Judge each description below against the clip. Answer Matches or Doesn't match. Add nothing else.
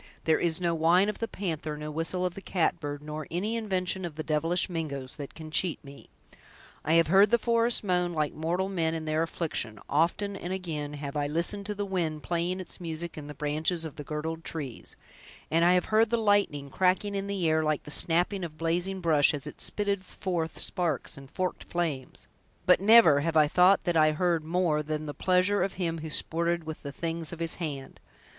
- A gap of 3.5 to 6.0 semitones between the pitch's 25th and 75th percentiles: Doesn't match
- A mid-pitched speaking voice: Matches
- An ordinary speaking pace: Doesn't match